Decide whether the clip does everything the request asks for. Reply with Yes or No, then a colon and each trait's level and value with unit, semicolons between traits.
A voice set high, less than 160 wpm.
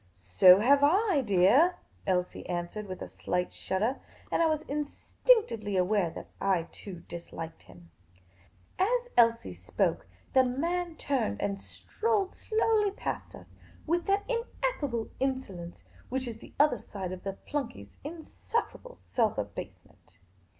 Yes: high, 240 Hz; slow, 135 wpm